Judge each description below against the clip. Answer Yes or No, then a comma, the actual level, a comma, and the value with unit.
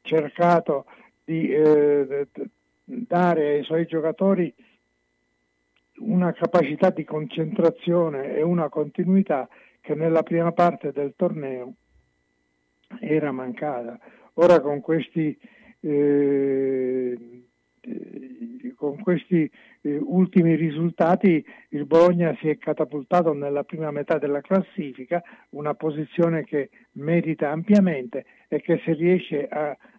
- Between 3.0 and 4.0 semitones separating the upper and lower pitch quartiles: Yes, average, 3.3 semitones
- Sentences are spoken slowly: Yes, slow, 100 wpm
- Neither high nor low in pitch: Yes, medium, 155 Hz